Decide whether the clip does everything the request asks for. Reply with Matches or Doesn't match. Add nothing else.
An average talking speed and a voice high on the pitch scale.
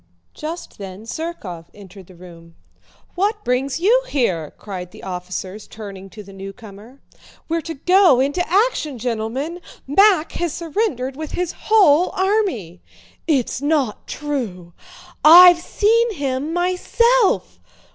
Doesn't match